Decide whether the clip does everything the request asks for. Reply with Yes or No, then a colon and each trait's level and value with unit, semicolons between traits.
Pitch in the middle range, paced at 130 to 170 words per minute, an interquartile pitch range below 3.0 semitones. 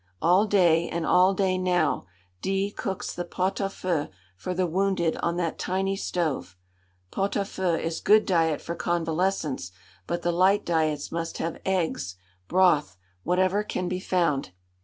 Yes: medium, 180 Hz; average, 160 wpm; narrow, 2.5 semitones